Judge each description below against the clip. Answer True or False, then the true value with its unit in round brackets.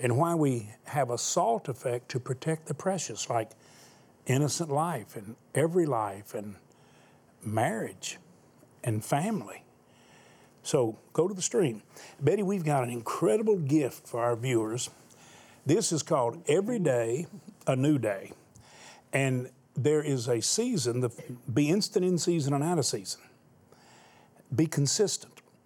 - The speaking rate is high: False (140 wpm)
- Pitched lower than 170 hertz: True (140 Hz)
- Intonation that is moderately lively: False (5.9 semitones)